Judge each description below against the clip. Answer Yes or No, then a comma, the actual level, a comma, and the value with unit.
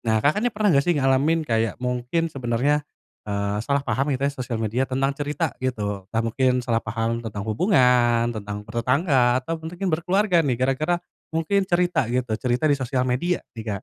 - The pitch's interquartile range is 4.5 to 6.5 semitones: Yes, average, 5.0 semitones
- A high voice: No, low, 130 Hz